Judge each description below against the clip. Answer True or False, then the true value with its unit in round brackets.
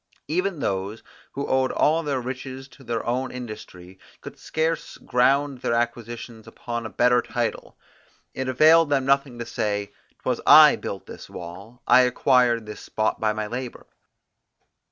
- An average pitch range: True (3.1 semitones)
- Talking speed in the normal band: True (155 wpm)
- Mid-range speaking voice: False (125 Hz)